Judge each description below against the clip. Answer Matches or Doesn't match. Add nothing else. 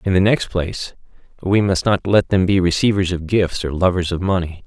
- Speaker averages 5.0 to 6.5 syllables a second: Matches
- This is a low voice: Matches